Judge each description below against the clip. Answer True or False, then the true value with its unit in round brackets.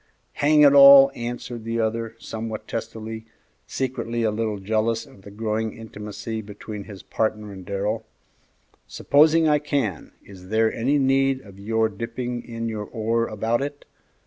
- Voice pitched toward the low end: True (115 Hz)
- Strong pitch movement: False (2.4 semitones)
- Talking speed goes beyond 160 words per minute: False (150 wpm)